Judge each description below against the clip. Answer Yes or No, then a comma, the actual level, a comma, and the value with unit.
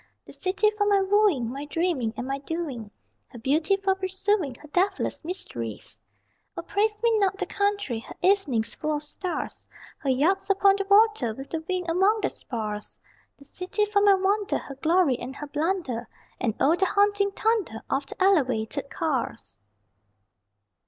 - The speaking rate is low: No, average, 165 wpm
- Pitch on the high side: Yes, very high, 350 Hz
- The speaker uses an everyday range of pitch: No, wide, 6.8 semitones